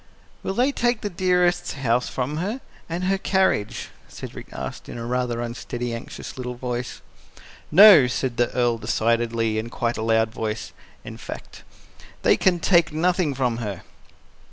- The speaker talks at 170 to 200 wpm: No, average, 155 wpm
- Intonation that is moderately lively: No, wide, 7.2 semitones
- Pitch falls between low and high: No, low, 125 Hz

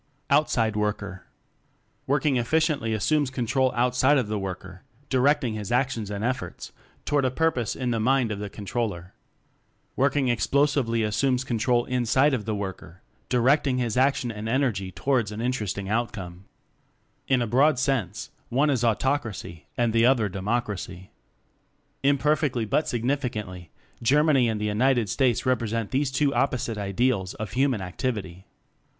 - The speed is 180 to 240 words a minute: No, average, 150 wpm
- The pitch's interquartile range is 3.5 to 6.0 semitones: Yes, average, 4.1 semitones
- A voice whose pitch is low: Yes, low, 120 Hz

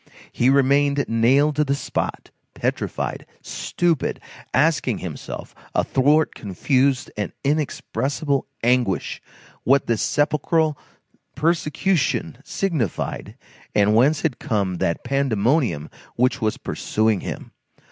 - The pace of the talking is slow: Yes, slow, 100 wpm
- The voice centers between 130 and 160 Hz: Yes, low, 135 Hz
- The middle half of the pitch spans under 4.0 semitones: No, average, 4.6 semitones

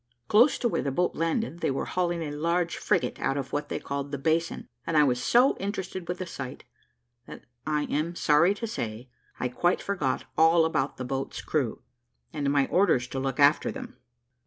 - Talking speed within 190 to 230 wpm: Yes, average, 200 wpm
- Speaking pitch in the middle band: Yes, medium, 155 Hz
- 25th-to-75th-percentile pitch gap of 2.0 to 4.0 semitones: No, average, 4.4 semitones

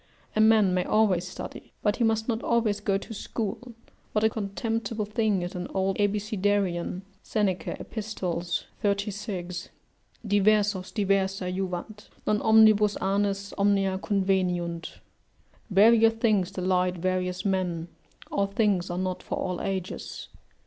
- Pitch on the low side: No, high, 200 Hz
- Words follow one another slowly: Yes, slow, 130 wpm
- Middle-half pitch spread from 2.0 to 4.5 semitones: Yes, narrow, 2.5 semitones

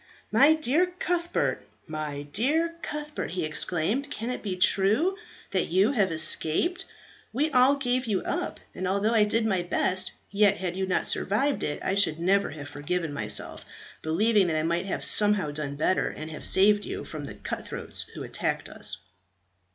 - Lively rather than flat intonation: Yes, wide, 7.4 semitones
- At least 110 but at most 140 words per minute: No, average, 175 wpm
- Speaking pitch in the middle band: No, high, 195 Hz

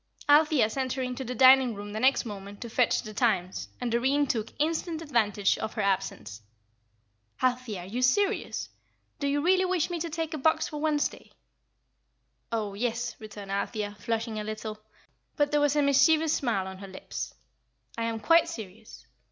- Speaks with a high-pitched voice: Yes, high, 245 Hz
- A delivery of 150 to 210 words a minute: Yes, average, 175 wpm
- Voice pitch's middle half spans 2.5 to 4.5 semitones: No, wide, 5.5 semitones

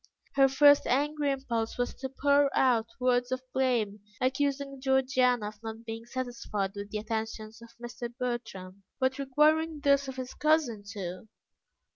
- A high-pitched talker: Yes, very high, 250 Hz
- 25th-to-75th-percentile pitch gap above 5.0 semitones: No, average, 3.6 semitones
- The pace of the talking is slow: No, average, 150 wpm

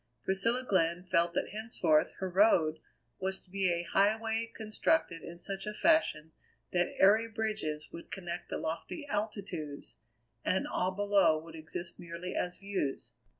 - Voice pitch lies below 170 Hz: No, high, 190 Hz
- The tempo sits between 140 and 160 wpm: Yes, average, 150 wpm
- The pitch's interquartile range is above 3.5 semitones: Yes, average, 3.9 semitones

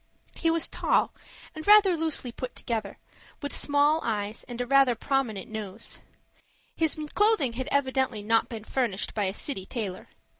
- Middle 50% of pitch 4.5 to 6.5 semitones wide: Yes, average, 5.0 semitones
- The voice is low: No, very high, 250 Hz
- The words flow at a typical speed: Yes, average, 155 wpm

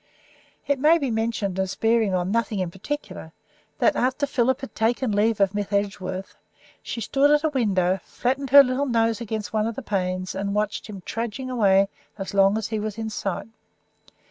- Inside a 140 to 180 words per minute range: No, average, 190 wpm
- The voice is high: Yes, high, 220 Hz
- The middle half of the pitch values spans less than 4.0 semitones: No, average, 4.3 semitones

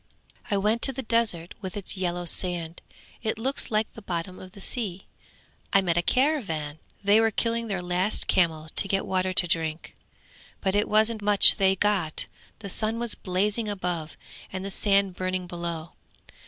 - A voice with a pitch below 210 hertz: Yes, high, 190 Hz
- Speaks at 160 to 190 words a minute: Yes, average, 175 wpm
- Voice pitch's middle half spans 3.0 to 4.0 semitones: Yes, average, 3.3 semitones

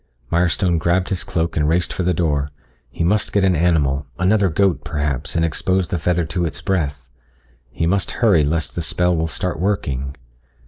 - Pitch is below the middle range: Yes, very low, 85 Hz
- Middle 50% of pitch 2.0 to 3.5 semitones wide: Yes, average, 2.9 semitones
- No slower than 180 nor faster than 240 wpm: Yes, average, 185 wpm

